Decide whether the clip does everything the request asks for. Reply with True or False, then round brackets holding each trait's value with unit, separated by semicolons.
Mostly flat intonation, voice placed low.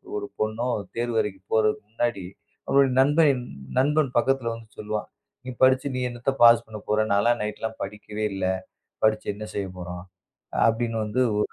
False (3.3 semitones; 115 Hz)